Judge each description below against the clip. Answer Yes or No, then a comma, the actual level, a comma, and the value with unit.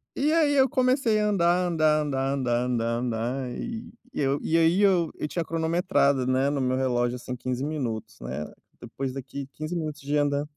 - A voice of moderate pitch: Yes, medium, 145 Hz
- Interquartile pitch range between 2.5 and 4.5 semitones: No, average, 5.2 semitones